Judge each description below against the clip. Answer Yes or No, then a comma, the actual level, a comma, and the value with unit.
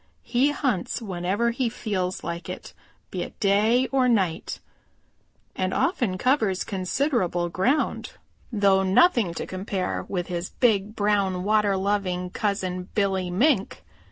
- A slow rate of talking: Yes, slow, 130 wpm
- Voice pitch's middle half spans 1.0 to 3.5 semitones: No, average, 4.2 semitones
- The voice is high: Yes, high, 200 Hz